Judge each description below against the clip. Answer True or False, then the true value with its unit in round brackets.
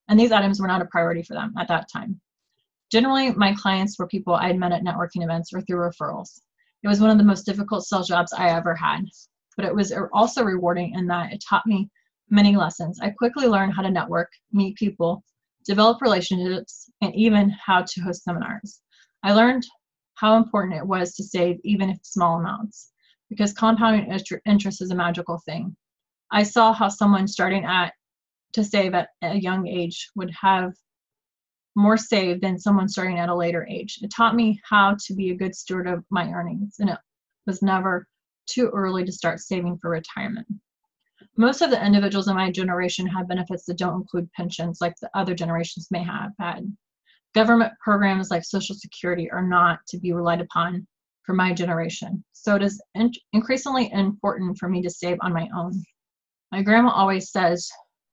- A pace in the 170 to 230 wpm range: True (190 wpm)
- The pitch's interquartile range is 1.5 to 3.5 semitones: True (2.8 semitones)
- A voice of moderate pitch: False (195 Hz)